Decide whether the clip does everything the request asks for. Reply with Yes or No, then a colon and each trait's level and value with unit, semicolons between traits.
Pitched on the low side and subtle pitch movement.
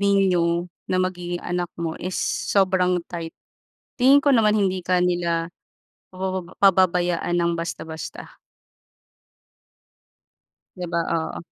No: medium, 180 Hz; narrow, 1.6 semitones